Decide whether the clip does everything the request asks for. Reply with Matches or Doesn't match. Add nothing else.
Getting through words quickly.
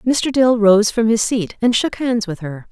Matches